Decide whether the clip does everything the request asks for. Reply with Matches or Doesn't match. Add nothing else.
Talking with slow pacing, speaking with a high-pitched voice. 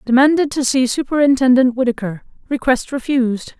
Matches